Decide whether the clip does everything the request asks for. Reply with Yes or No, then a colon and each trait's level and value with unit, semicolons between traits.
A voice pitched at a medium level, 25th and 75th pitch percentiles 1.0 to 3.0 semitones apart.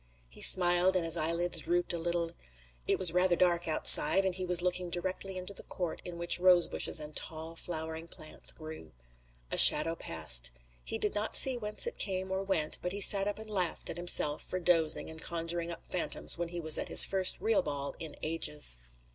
Yes: medium, 175 Hz; narrow, 2.4 semitones